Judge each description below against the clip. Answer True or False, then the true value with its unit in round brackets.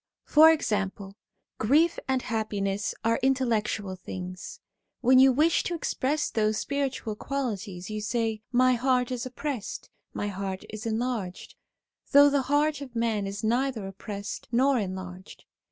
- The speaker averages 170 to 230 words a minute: False (145 wpm)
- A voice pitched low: False (230 Hz)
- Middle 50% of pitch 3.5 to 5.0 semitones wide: True (4.6 semitones)